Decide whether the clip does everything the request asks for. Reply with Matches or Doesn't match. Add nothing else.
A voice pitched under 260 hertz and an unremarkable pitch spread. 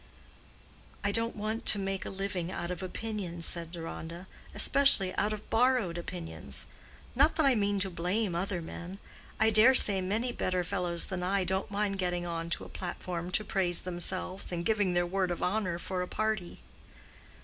Matches